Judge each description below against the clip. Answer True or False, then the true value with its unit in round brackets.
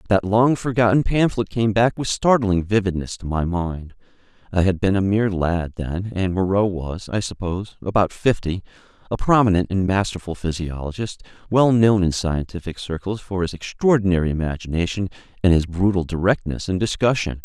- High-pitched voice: False (95 Hz)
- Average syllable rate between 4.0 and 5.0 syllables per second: False (5.3 syllables/s)